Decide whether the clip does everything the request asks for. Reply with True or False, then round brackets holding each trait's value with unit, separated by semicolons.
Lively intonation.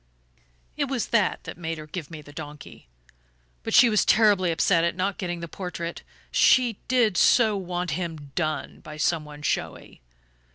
False (4.6 semitones)